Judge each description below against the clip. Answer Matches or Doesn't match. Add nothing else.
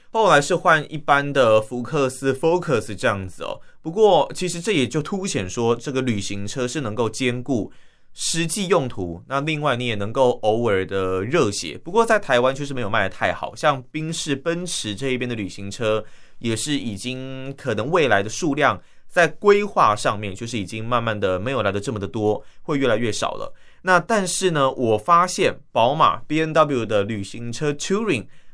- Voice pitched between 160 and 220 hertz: Doesn't match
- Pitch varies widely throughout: Matches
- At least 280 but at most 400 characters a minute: Matches